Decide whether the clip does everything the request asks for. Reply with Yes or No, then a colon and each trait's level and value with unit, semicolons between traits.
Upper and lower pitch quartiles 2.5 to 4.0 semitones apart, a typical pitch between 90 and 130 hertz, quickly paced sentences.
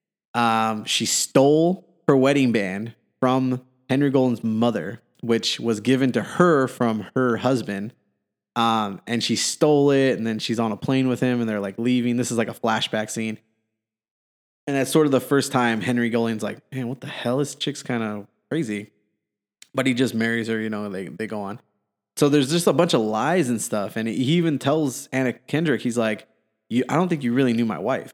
Yes: average, 3.3 semitones; low, 120 Hz; fast, 210 wpm